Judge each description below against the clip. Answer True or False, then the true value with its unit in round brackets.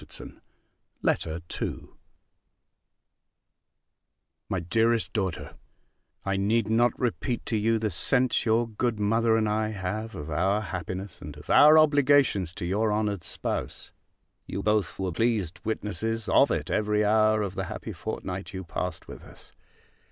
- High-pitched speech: False (105 Hz)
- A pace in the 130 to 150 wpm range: True (145 wpm)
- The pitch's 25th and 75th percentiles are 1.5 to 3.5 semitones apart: True (2.9 semitones)